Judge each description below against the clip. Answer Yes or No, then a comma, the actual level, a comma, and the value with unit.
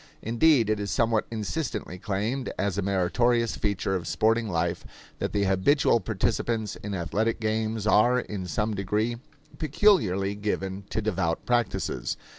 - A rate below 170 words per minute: Yes, average, 140 wpm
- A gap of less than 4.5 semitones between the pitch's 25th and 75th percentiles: Yes, average, 3.2 semitones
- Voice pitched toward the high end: No, low, 105 Hz